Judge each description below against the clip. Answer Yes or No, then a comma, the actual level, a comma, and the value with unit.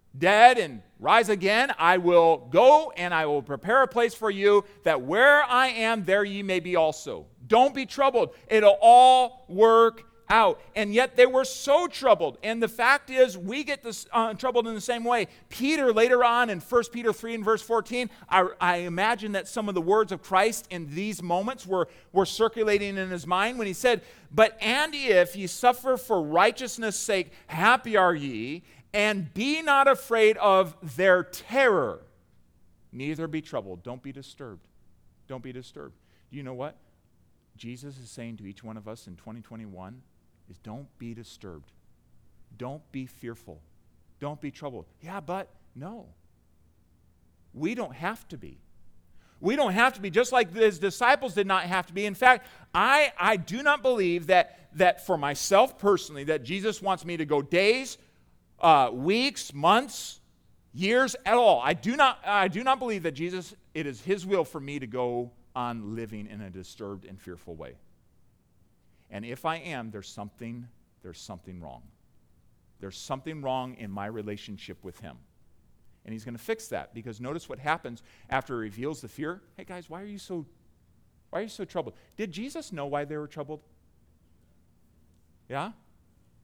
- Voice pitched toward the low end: No, medium, 180 Hz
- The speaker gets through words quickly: No, average, 180 wpm